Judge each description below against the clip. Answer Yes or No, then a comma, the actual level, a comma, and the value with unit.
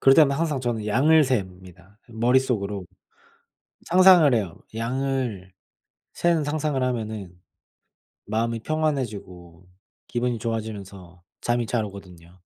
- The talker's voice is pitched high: No, low, 115 Hz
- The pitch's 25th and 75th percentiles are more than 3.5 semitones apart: Yes, wide, 5.5 semitones